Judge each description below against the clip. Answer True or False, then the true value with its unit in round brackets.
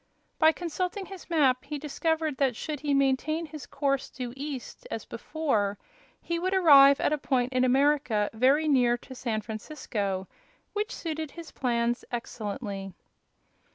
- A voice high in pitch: True (275 Hz)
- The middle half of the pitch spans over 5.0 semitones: False (4.5 semitones)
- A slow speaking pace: False (150 wpm)